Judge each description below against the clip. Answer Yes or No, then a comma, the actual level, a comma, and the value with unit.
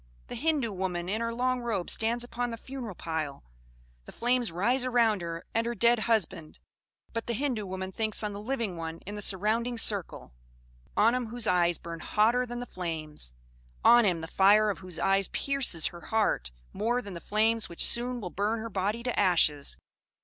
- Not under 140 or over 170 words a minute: No, average, 195 wpm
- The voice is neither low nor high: No, high, 215 Hz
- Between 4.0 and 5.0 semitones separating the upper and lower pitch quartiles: Yes, average, 4.7 semitones